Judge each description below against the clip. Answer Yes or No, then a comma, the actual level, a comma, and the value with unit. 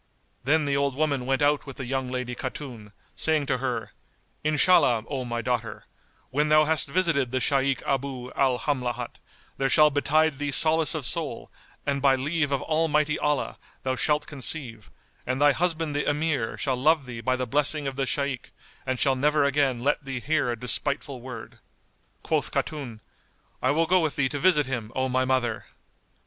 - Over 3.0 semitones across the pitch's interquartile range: No, average, 2.7 semitones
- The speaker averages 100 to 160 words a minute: No, average, 185 wpm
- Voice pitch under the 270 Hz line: Yes, medium, 140 Hz